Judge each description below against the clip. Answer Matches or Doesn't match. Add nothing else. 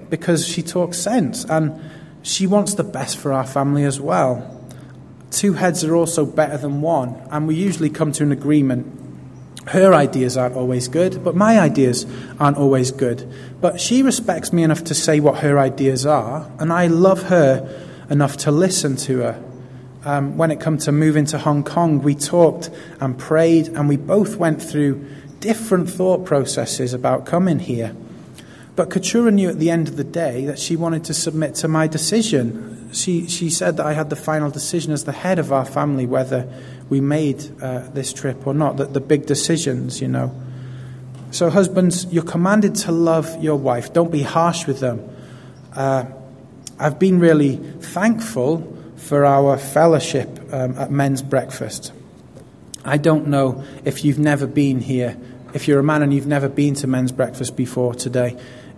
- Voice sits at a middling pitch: Matches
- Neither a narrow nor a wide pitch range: Matches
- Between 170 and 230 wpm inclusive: Matches